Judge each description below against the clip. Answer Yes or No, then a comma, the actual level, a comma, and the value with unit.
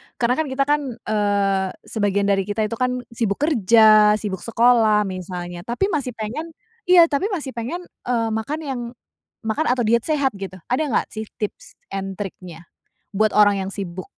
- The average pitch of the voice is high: Yes, high, 220 Hz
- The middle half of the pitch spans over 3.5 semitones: Yes, average, 4.1 semitones